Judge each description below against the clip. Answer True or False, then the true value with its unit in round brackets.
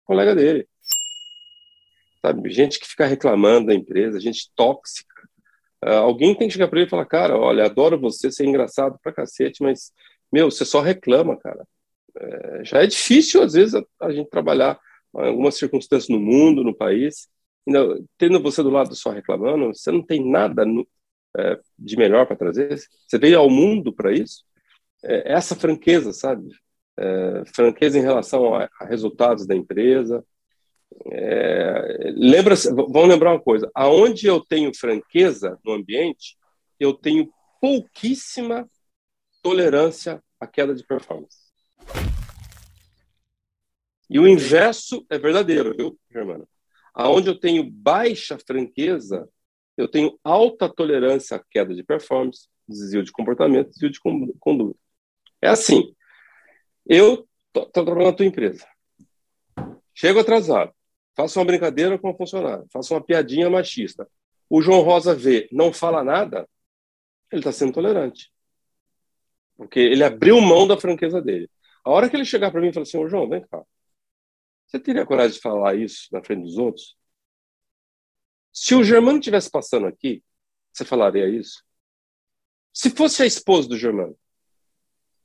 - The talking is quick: False (150 wpm)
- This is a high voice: False (175 Hz)